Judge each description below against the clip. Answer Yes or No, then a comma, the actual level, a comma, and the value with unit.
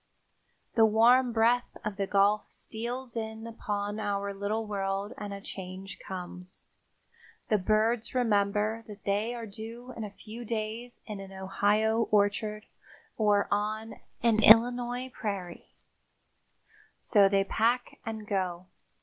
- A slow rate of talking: Yes, slow, 130 wpm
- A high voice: Yes, high, 215 Hz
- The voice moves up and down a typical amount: No, narrow, 2.1 semitones